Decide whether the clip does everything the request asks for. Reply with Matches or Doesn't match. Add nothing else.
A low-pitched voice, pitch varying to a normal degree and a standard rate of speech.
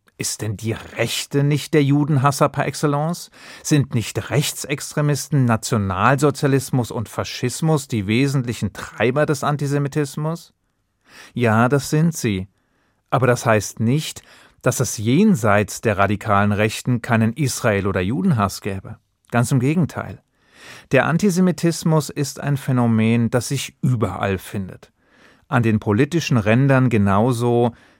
Doesn't match